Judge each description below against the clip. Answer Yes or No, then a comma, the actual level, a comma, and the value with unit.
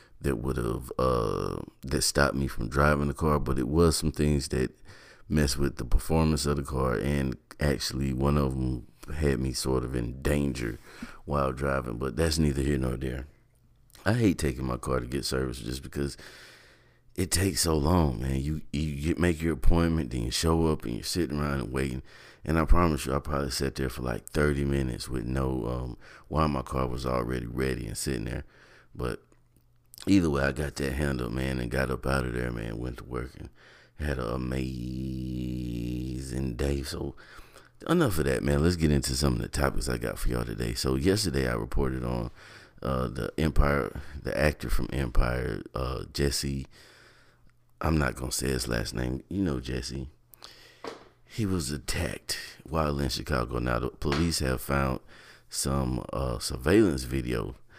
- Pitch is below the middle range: Yes, very low, 70 Hz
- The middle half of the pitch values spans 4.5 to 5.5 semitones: No, average, 2.8 semitones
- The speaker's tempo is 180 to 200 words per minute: Yes, average, 185 wpm